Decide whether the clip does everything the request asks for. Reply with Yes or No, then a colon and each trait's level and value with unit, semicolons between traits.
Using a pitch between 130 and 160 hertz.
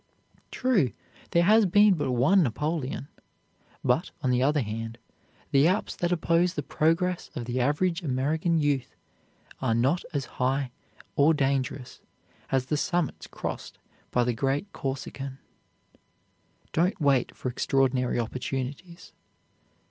Yes: medium, 140 Hz